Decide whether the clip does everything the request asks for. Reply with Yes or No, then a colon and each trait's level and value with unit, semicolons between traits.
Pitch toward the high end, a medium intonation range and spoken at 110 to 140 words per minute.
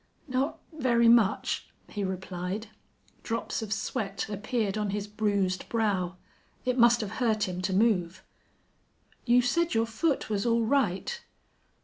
Yes: high, 215 Hz; average, 3.4 semitones; slow, 135 wpm